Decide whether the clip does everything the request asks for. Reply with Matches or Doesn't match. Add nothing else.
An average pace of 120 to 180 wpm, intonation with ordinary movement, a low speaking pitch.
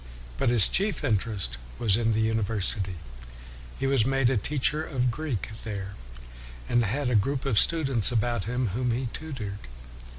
Matches